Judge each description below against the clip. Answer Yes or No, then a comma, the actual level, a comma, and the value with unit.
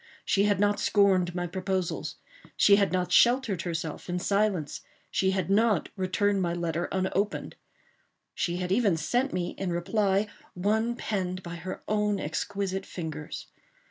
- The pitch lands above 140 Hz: Yes, high, 190 Hz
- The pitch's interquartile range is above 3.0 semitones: No, narrow, 2.5 semitones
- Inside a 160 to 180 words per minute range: No, average, 145 wpm